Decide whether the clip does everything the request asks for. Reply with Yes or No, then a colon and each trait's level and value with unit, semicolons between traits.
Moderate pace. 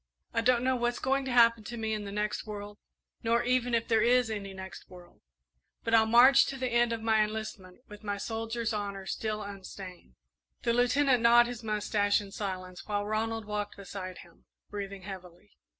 Yes: average, 190 wpm